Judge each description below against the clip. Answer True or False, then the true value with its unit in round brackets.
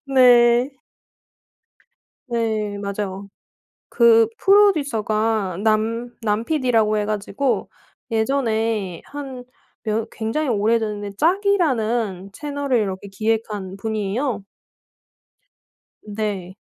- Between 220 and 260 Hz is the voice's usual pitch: True (225 Hz)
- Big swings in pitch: False (3.3 semitones)